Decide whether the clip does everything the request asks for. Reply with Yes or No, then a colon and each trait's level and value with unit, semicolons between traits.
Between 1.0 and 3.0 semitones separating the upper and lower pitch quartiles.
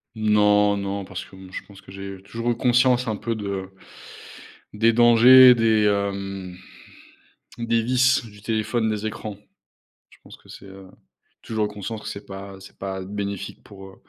Yes: average, 2.7 semitones